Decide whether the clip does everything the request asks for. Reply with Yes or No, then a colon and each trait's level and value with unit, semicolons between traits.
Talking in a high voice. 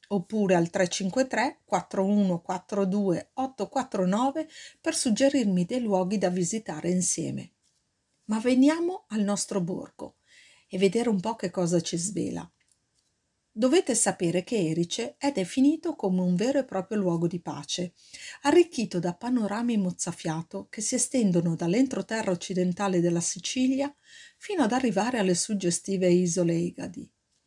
Yes: high, 200 Hz